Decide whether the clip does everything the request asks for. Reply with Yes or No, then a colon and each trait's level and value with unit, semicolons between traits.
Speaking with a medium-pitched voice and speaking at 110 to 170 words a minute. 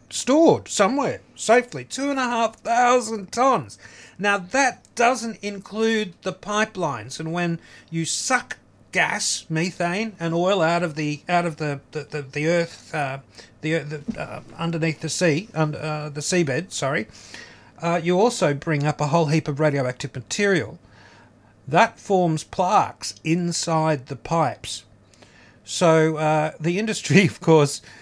Yes: medium, 160 Hz; average, 145 wpm